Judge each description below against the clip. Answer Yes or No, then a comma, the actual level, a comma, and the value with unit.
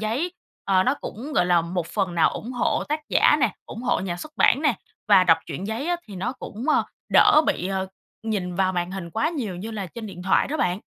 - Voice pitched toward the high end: Yes, high, 200 Hz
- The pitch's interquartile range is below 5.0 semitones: No, wide, 5.5 semitones